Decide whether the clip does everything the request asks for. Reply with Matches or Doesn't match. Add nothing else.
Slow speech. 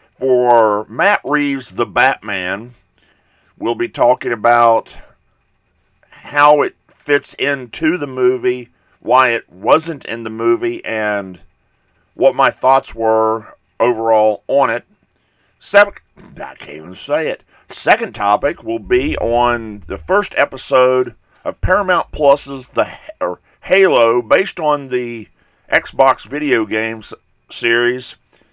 Matches